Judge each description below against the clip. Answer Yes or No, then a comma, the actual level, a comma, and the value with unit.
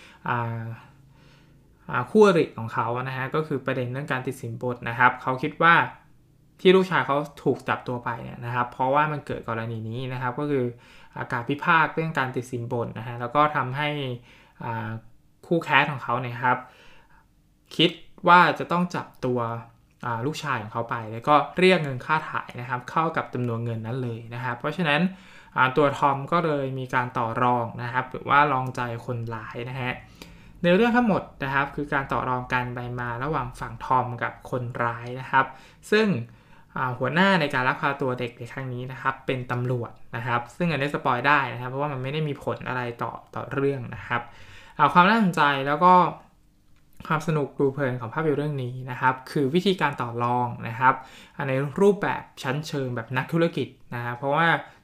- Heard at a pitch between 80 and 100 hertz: No, low, 130 Hz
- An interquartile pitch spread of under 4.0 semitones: Yes, average, 3.4 semitones